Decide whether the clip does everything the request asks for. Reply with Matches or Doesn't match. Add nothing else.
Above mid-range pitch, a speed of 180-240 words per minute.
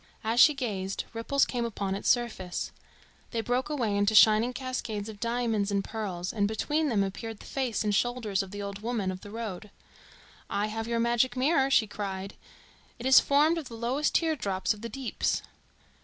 Matches